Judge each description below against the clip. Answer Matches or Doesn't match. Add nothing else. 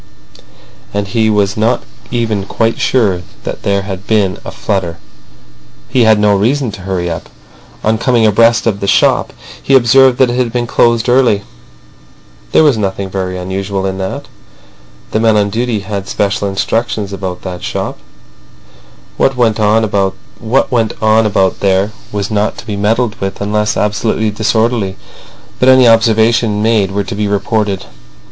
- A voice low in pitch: Matches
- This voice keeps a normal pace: Matches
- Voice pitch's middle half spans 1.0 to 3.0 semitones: Matches